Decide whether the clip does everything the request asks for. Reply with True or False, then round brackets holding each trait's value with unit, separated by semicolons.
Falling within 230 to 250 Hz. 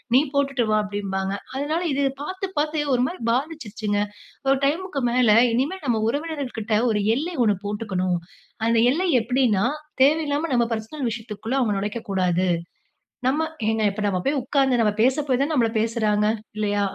True (240 Hz)